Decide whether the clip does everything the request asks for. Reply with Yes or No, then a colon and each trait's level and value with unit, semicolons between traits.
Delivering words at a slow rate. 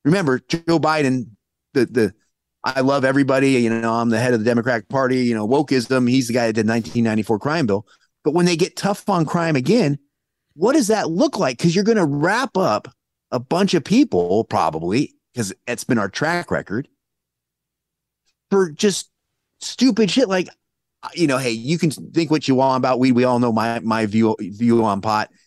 No: fast, 205 wpm